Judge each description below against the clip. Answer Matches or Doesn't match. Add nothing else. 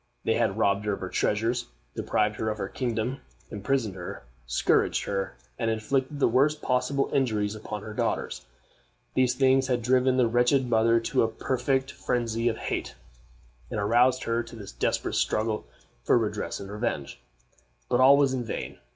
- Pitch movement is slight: Doesn't match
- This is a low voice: Matches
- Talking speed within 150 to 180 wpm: Matches